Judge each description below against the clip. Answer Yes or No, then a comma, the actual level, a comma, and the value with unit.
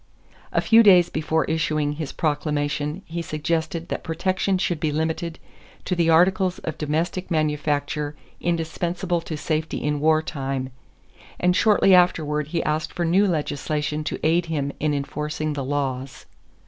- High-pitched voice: No, medium, 155 Hz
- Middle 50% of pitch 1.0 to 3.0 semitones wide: Yes, narrow, 2.5 semitones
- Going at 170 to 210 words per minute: No, average, 145 wpm